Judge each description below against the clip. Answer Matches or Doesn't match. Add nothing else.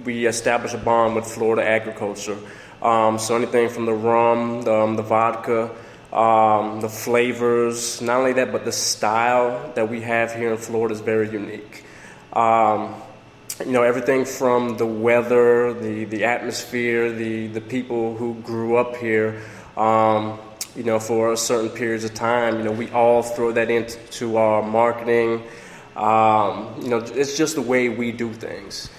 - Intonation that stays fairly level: Matches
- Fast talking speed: Doesn't match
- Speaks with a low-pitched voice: Matches